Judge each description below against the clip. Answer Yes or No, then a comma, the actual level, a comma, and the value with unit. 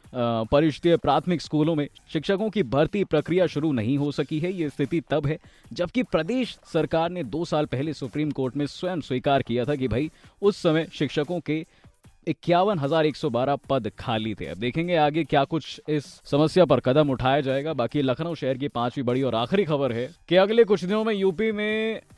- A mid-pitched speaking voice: Yes, medium, 155 Hz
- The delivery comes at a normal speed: Yes, average, 180 wpm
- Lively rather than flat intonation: No, average, 4.2 semitones